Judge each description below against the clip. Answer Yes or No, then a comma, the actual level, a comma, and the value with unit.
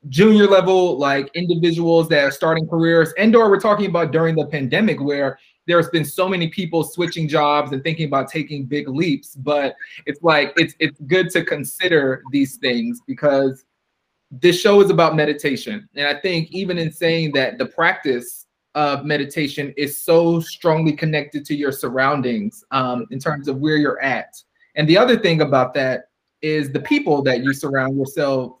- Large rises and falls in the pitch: No, average, 3.2 semitones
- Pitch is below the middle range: No, medium, 155 Hz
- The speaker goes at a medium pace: Yes, average, 175 wpm